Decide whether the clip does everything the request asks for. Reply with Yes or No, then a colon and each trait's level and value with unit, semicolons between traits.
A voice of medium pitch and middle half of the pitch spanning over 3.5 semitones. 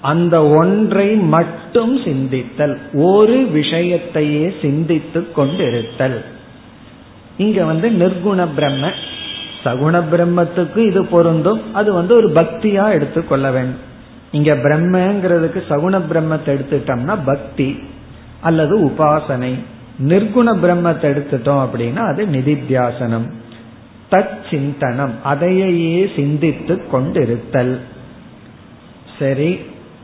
Yes: medium, 155 Hz; average, 4.8 semitones